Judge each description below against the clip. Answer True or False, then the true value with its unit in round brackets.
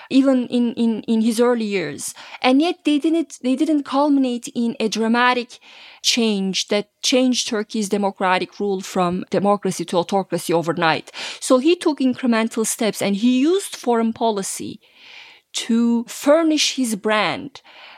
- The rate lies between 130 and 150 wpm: True (140 wpm)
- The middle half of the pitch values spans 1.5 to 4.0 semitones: False (4.5 semitones)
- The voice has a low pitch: False (235 Hz)